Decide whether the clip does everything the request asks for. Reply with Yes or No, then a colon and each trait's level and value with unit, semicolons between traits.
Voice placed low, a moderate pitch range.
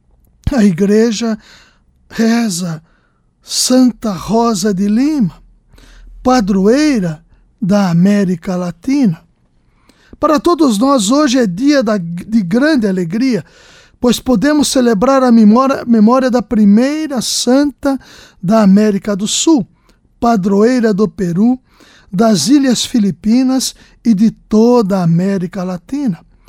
No: high, 225 Hz; average, 4.5 semitones